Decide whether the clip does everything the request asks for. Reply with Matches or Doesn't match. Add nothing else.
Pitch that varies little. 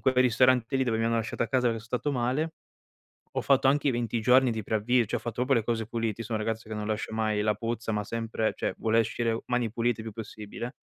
Matches